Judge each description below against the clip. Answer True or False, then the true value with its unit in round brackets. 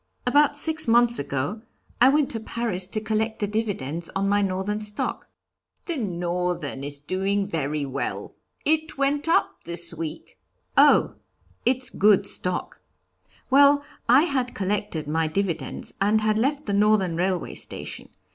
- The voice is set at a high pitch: True (205 Hz)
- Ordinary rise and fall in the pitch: False (5.9 semitones)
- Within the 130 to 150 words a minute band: True (145 wpm)